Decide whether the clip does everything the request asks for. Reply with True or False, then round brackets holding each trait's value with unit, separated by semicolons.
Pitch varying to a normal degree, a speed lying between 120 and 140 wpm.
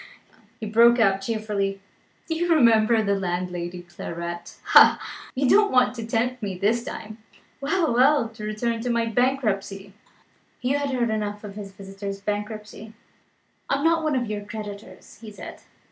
False (3.7 semitones; 160 wpm)